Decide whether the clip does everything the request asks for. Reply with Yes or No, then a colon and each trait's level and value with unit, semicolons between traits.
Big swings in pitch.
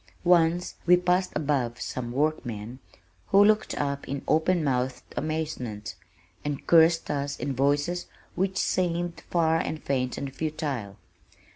No: average, 4.3 semitones